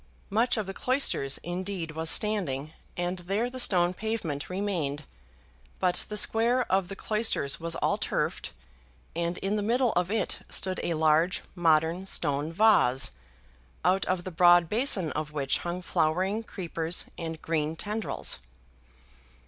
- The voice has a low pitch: No, medium, 180 Hz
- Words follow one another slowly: No, average, 145 wpm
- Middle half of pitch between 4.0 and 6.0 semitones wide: Yes, average, 4.3 semitones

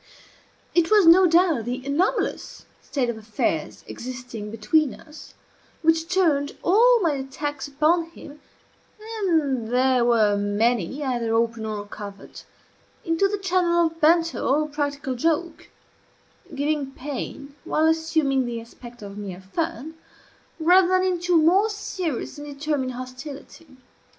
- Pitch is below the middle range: No, very high, 290 Hz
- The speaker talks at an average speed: No, slow, 130 wpm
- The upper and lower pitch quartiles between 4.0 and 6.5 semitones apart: Yes, average, 5.3 semitones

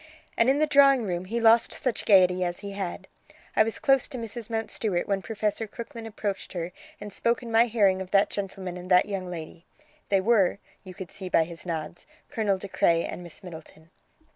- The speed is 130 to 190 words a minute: No, fast, 205 wpm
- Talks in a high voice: Yes, high, 200 Hz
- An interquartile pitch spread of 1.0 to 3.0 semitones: No, average, 3.8 semitones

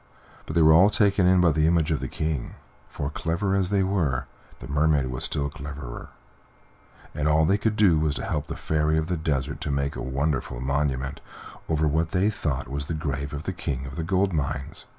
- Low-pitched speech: Yes, very low, 75 Hz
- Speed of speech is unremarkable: No, fast, 215 wpm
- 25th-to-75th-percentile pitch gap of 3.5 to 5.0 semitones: No, average, 3.1 semitones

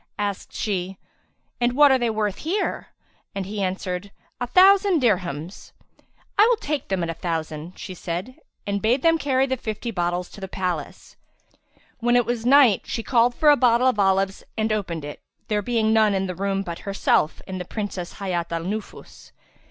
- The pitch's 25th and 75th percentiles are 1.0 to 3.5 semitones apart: No, average, 5.0 semitones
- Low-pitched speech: No, high, 205 Hz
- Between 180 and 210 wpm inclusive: Yes, average, 185 wpm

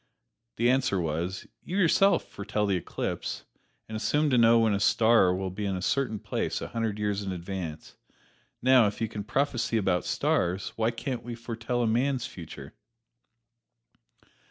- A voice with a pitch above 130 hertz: No, low, 110 Hz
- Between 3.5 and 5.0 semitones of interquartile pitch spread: Yes, average, 4.0 semitones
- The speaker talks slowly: No, average, 165 wpm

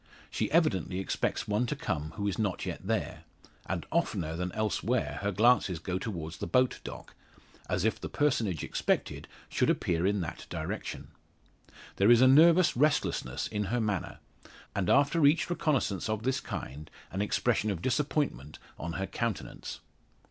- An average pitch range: No, wide, 6.1 semitones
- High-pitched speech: No, low, 105 Hz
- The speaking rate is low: No, average, 160 wpm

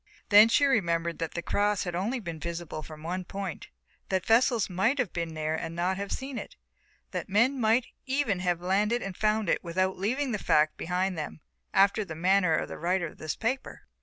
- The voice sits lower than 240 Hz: Yes, high, 190 Hz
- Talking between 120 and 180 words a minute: No, fast, 205 wpm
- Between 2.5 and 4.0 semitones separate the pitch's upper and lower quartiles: No, average, 4.4 semitones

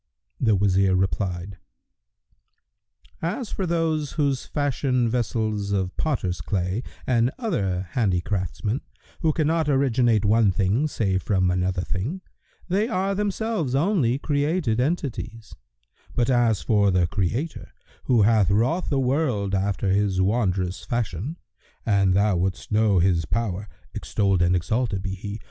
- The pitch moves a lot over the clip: Yes, wide, 6.5 semitones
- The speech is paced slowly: Yes, slow, 130 wpm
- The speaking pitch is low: Yes, low, 110 Hz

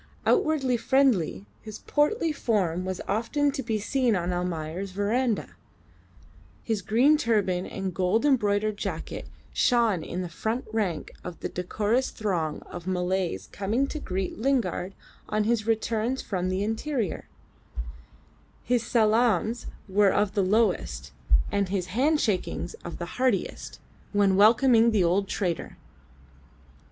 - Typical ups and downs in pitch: Yes, average, 4.3 semitones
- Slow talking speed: Yes, slow, 130 wpm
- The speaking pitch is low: No, high, 210 Hz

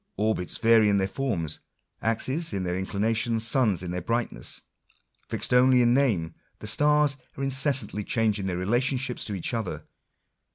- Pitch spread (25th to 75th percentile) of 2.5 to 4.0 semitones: No, average, 5.1 semitones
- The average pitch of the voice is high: No, low, 115 Hz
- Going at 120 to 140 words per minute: No, average, 160 wpm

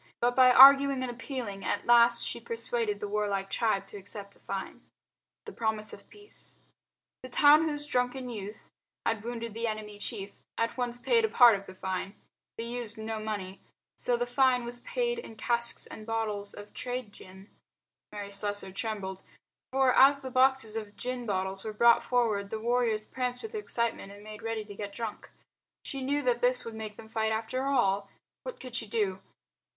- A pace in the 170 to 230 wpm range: Yes, average, 185 wpm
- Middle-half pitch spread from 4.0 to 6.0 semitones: No, average, 3.5 semitones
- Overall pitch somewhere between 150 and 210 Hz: No, high, 230 Hz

